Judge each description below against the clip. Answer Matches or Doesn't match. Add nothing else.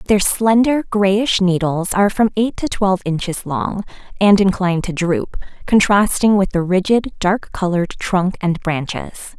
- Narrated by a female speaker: Matches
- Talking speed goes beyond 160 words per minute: Doesn't match